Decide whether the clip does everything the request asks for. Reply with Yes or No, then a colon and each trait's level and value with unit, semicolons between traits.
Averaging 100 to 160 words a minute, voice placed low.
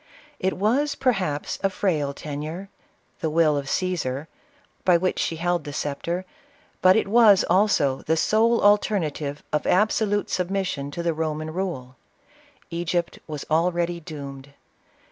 No: average, 145 wpm; medium, 170 Hz